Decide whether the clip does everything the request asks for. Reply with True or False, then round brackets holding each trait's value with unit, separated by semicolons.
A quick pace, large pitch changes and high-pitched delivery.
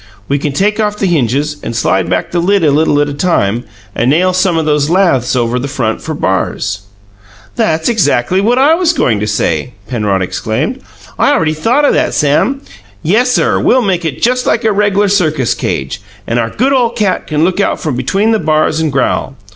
False (210 wpm; 8.2 semitones; 160 Hz)